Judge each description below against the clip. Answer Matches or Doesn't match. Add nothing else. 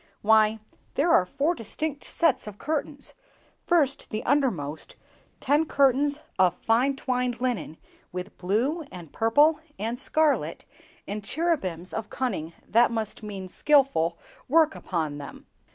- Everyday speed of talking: Doesn't match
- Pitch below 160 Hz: Doesn't match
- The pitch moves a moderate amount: Doesn't match